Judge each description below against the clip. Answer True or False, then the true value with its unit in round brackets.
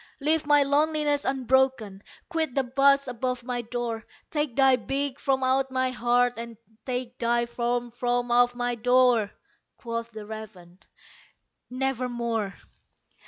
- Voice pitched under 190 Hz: False (245 Hz)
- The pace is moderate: False (130 wpm)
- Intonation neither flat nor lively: False (2.2 semitones)